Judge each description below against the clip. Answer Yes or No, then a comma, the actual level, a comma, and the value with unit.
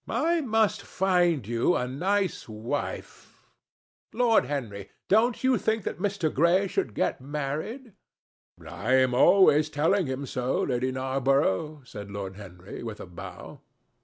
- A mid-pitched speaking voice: Yes, medium, 145 Hz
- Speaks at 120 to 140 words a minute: Yes, slow, 135 wpm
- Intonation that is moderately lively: No, wide, 8.2 semitones